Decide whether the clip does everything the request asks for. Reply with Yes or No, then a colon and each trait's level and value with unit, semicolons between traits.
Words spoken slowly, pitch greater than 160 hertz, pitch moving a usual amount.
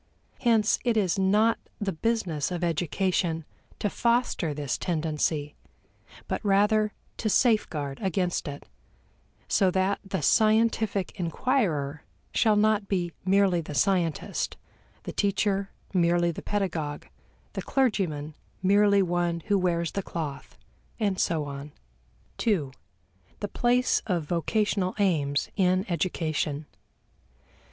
Yes: slow, 115 wpm; medium, 185 Hz; average, 4.4 semitones